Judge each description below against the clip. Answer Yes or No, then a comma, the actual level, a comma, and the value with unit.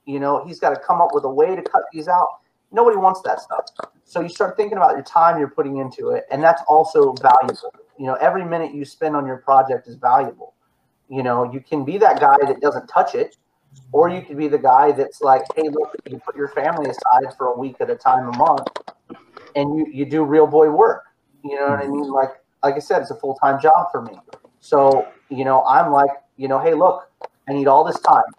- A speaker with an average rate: No, fast, 240 wpm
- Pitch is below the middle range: No, medium, 150 Hz